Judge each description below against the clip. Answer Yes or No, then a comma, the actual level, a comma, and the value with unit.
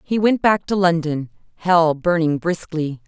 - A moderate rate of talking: Yes, average, 155 wpm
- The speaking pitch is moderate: Yes, medium, 170 Hz